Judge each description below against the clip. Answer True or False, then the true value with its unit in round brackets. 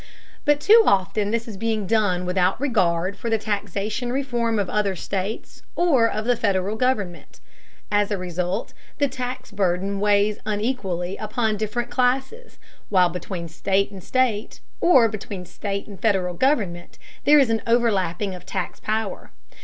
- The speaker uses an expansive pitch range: False (3.7 semitones)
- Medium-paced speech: True (155 wpm)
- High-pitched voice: True (210 Hz)